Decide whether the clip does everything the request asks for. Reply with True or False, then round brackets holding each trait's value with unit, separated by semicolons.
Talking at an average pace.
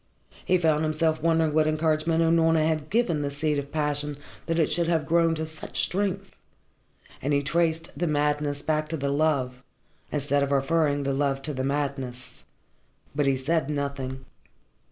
True (170 wpm)